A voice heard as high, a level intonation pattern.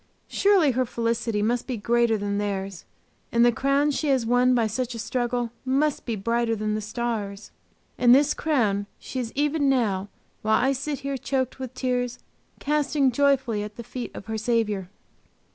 No: high, 240 Hz; average, 3.5 semitones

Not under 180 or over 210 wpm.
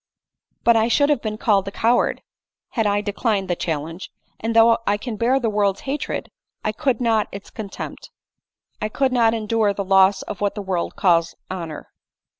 Yes: average, 195 wpm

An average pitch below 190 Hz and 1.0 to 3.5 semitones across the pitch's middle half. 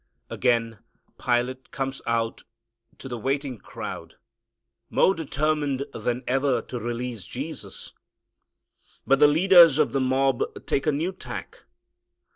Yes: low, 135 Hz; average, 3.1 semitones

